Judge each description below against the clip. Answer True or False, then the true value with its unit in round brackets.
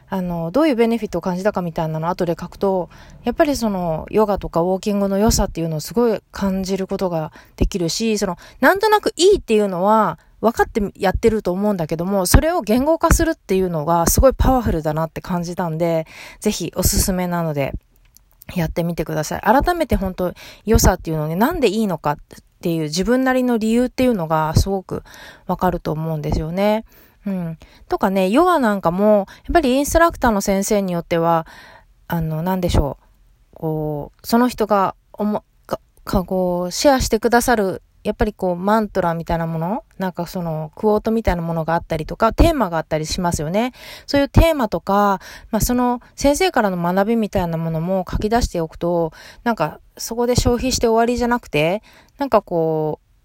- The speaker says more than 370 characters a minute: True (410 characters per minute)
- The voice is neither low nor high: False (195 Hz)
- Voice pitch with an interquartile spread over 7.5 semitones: False (5.2 semitones)